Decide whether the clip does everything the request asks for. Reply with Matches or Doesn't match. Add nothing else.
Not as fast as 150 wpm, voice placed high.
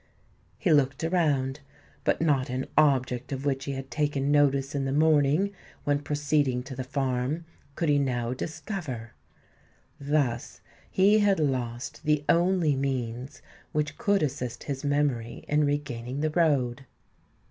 Doesn't match